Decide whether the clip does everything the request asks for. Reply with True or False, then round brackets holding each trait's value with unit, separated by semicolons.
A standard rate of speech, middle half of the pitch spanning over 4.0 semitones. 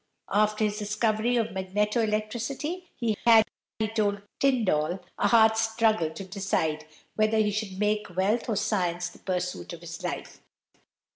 False (150 wpm; 2.8 semitones)